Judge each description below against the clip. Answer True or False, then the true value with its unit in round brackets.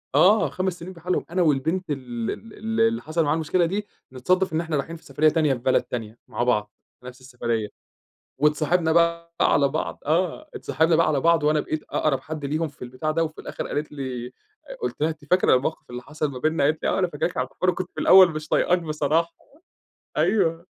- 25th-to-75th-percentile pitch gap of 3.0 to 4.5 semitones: True (3.5 semitones)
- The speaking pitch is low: False (155 Hz)